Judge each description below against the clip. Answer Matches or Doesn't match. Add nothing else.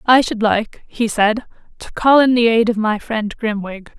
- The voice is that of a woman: Matches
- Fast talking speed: Matches